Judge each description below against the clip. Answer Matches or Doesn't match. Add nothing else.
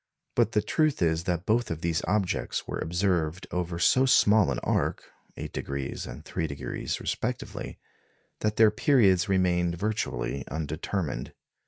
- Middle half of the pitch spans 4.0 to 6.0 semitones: Matches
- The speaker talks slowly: Matches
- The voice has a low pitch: Matches